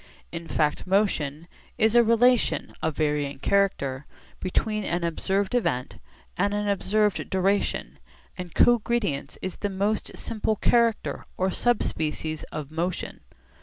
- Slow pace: Yes, slow, 125 wpm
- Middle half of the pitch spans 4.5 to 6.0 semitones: Yes, average, 5.2 semitones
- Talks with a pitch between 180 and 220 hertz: Yes, high, 190 Hz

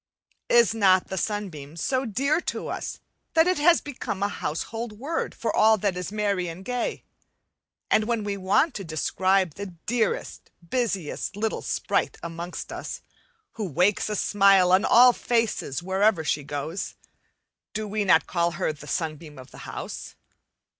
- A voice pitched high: Yes, high, 200 Hz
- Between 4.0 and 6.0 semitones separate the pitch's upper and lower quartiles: Yes, average, 4.6 semitones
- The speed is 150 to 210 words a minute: Yes, average, 160 wpm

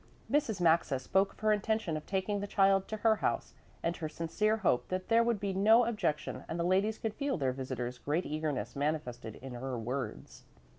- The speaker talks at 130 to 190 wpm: No, average, 200 wpm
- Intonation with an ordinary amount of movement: No, wide, 7.3 semitones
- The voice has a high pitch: No, medium, 180 Hz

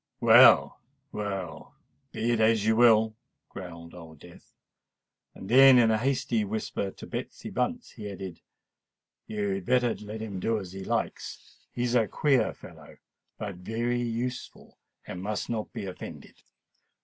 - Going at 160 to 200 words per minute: No, average, 140 wpm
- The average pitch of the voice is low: Yes, low, 110 Hz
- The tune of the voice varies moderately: Yes, average, 3.5 semitones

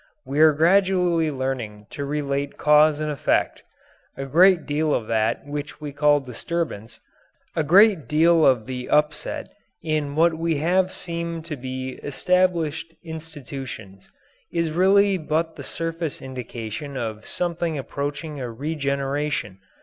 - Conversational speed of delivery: No, slow, 130 wpm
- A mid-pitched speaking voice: Yes, medium, 150 Hz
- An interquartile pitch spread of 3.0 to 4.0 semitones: Yes, average, 3.5 semitones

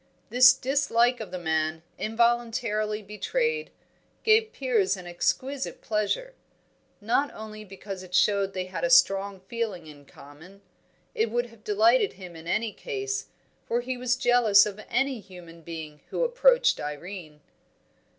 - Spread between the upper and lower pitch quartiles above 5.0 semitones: Yes, wide, 5.4 semitones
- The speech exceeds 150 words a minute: No, average, 140 wpm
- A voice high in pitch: Yes, high, 215 Hz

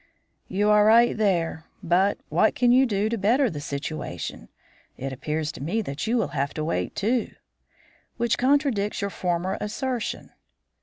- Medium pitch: No, high, 205 Hz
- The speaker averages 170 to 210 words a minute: No, average, 160 wpm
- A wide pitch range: Yes, wide, 6.3 semitones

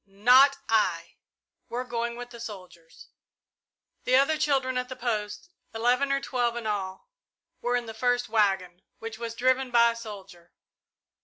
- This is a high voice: Yes, high, 235 Hz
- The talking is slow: No, average, 155 wpm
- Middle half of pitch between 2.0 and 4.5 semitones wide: Yes, average, 2.8 semitones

